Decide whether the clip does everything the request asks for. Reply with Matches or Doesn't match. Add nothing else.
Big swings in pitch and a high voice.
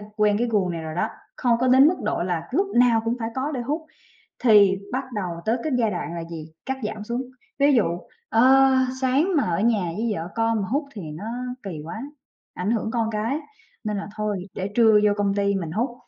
Doesn't match